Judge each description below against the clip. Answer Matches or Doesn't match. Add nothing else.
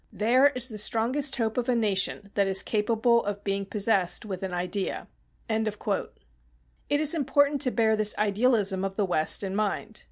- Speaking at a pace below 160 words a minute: Doesn't match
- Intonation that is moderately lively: Matches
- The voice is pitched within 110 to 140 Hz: Doesn't match